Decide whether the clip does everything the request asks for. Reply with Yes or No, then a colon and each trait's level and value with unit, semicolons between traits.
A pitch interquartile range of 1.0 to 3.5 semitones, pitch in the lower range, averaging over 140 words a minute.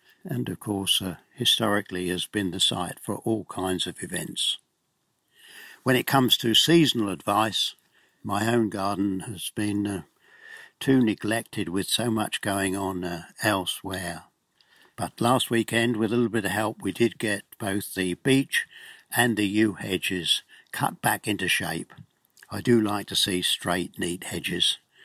Yes: average, 3.1 semitones; low, 105 Hz; average, 160 wpm